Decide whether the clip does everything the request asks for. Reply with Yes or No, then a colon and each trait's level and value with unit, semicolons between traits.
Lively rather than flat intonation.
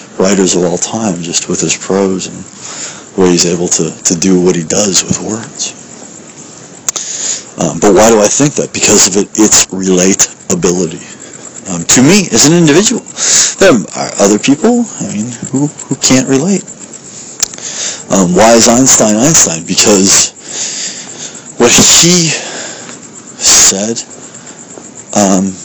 Yes: wide, 7.6 semitones